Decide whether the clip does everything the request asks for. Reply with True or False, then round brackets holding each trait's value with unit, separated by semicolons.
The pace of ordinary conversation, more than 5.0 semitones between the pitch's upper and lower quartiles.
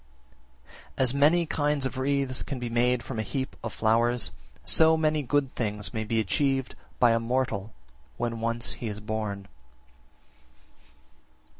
False (150 wpm; 3.5 semitones)